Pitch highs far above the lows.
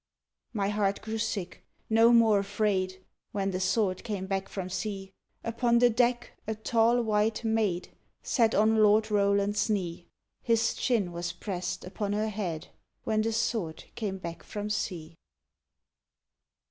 No: average, 2.7 semitones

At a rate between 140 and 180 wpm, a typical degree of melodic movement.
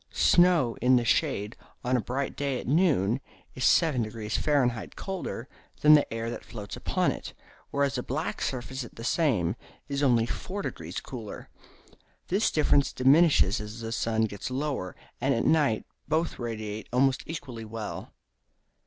Yes: average, 155 wpm; average, 4.4 semitones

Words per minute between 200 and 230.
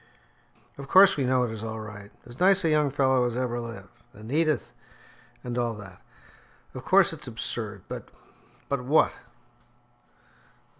No: average, 160 wpm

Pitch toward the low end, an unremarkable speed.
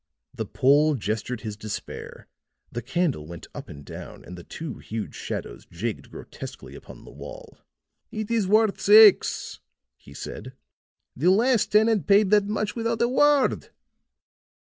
No: medium, 185 Hz; average, 145 wpm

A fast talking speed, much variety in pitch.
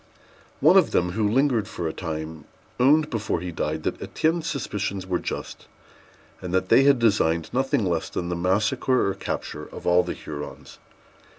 No: average, 175 wpm; wide, 6.2 semitones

